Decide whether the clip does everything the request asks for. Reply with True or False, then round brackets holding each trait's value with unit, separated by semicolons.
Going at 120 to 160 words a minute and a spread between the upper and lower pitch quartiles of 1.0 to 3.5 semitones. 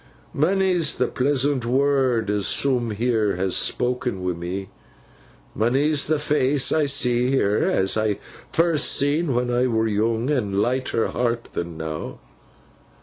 False (140 wpm; 4.8 semitones)